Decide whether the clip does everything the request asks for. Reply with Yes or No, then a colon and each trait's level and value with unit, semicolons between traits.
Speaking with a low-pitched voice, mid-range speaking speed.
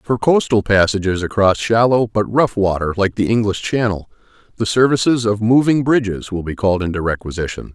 Yes: low, 110 Hz; average, 170 wpm